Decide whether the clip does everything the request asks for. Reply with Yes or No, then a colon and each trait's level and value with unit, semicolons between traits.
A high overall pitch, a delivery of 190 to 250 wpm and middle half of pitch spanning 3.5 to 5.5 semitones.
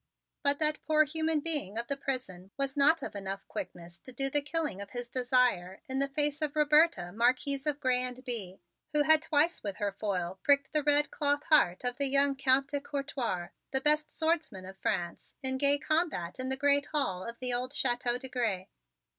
Yes: very high, 265 Hz; fast, 205 wpm; average, 4.3 semitones